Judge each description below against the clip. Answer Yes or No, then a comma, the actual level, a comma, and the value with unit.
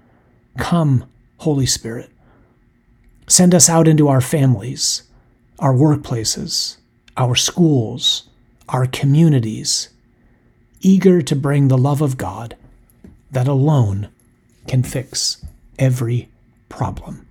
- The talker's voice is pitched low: Yes, low, 130 Hz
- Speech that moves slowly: Yes, slow, 95 wpm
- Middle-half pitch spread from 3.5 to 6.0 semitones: No, average, 3.0 semitones